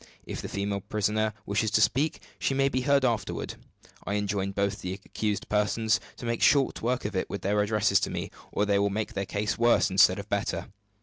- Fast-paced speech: Yes, fast, 210 wpm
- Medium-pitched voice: No, low, 105 Hz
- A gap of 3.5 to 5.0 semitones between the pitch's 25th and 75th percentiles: No, narrow, 2.5 semitones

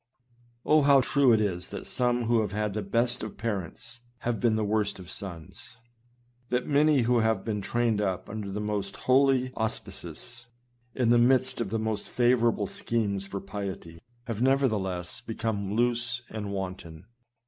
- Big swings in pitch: No, average, 3.4 semitones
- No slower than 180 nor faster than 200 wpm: No, average, 165 wpm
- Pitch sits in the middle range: No, low, 110 Hz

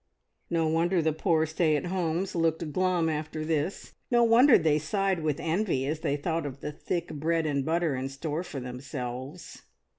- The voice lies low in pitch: No, medium, 160 Hz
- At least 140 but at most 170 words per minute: No, average, 180 wpm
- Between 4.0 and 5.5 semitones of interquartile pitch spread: No, average, 2.7 semitones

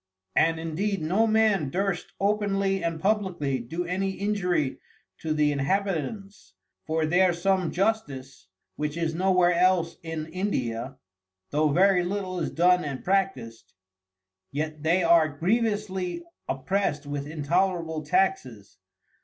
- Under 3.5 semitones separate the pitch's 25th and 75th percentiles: No, average, 4.2 semitones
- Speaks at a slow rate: Yes, slow, 125 wpm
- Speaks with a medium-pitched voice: Yes, medium, 175 Hz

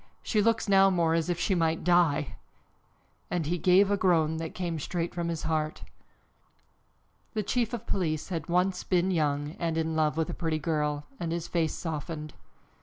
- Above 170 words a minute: Yes, average, 180 wpm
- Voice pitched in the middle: Yes, medium, 165 Hz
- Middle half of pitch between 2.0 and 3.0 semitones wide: Yes, narrow, 2.4 semitones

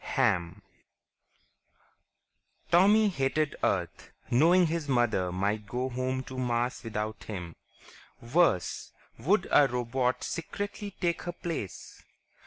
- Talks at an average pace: No, slow, 105 wpm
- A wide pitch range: Yes, wide, 7.6 semitones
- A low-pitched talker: Yes, low, 130 Hz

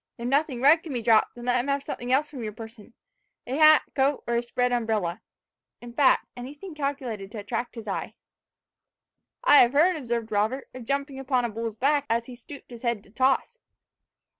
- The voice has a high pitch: Yes, high, 245 Hz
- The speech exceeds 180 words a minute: Yes, average, 200 wpm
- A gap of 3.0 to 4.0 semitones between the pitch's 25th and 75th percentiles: Yes, average, 3.4 semitones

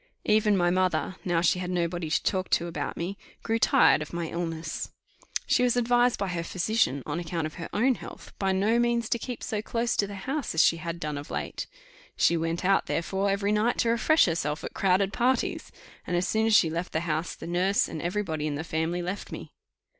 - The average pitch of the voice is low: No, medium, 180 Hz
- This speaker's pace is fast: Yes, fast, 225 wpm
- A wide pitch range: No, average, 4.2 semitones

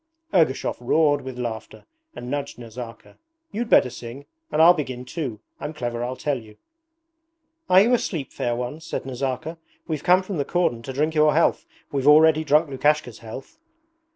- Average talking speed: Yes, average, 170 wpm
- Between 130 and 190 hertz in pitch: Yes, medium, 140 Hz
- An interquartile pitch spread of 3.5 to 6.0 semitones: Yes, average, 4.4 semitones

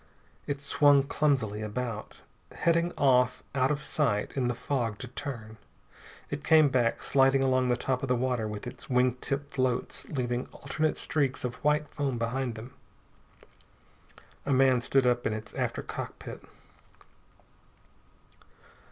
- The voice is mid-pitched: No, low, 130 Hz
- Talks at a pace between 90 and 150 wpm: Yes, average, 145 wpm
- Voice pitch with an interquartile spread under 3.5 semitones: Yes, narrow, 2.5 semitones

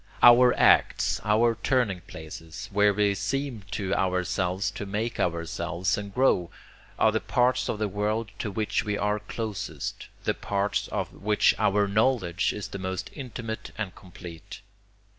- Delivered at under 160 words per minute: Yes, average, 150 wpm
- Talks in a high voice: No, low, 105 Hz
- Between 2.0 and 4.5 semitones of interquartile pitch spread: Yes, average, 3.0 semitones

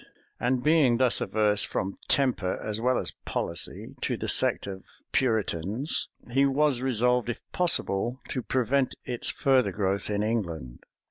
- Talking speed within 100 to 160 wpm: Yes, average, 145 wpm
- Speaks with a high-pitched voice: No, low, 120 Hz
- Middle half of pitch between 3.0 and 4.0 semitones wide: No, average, 4.4 semitones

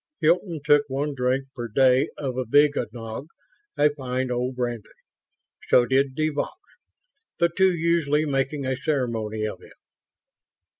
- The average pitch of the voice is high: No, low, 135 Hz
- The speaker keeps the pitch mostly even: No, average, 3.1 semitones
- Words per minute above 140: No, slow, 135 wpm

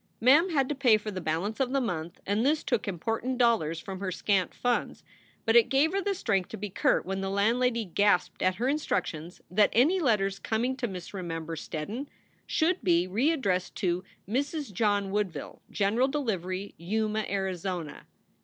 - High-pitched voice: Yes, high, 210 Hz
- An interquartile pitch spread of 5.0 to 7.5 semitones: Yes, average, 5.3 semitones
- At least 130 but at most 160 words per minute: No, average, 180 wpm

